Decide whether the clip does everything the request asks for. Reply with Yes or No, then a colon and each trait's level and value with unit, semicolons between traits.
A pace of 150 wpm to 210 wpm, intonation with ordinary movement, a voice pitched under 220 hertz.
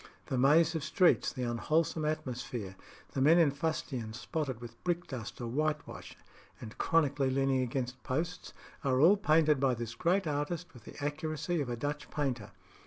Yes: average, 165 wpm; average, 4.1 semitones; medium, 140 Hz